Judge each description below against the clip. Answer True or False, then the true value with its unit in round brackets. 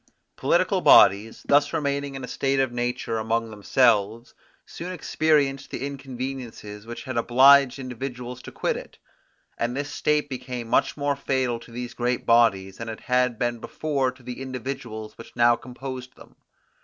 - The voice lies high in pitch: False (125 Hz)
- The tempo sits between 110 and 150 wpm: False (160 wpm)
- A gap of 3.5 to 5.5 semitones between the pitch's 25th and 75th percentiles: False (2.6 semitones)